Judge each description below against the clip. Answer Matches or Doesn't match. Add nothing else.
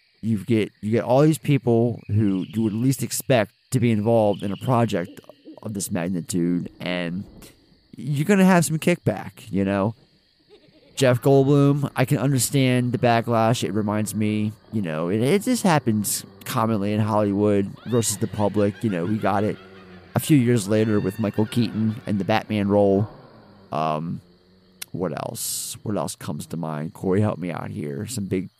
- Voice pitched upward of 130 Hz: Doesn't match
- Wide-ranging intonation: Doesn't match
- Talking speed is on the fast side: Doesn't match